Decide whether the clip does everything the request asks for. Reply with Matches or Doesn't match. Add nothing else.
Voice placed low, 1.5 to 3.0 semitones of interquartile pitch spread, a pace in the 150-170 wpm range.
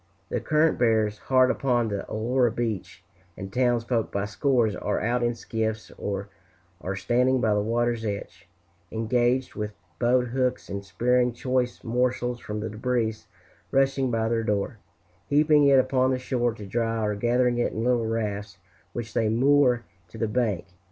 Matches